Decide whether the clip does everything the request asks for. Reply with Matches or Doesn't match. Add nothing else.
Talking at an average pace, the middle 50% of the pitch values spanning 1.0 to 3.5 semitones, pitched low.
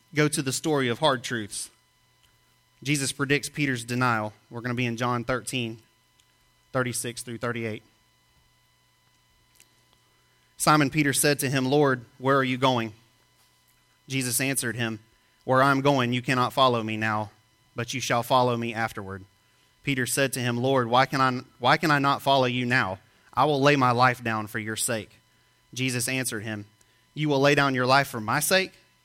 Matches